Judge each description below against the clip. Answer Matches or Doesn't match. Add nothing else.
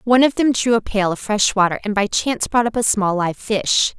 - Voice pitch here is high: Matches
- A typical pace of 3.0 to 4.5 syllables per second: Doesn't match